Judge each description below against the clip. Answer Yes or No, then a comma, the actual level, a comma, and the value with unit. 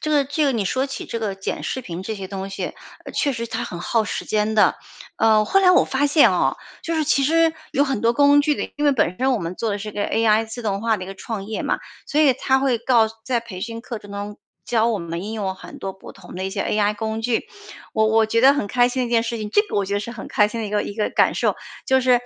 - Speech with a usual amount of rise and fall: Yes, average, 4.3 semitones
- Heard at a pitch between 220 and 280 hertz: Yes, high, 225 Hz